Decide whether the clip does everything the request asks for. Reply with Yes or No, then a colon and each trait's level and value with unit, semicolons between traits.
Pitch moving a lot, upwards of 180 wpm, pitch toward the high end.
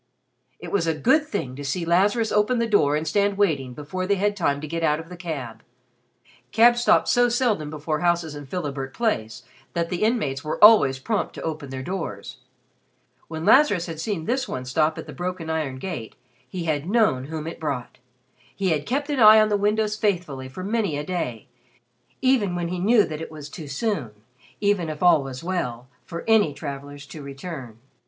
No: wide, 6.2 semitones; average, 200 wpm; medium, 165 Hz